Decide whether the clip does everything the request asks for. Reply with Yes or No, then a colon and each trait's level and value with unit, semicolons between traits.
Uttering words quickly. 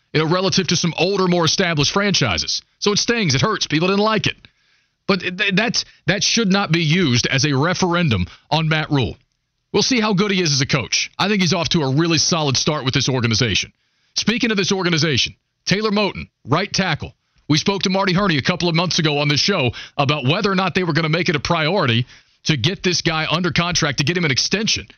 Yes: fast, 235 wpm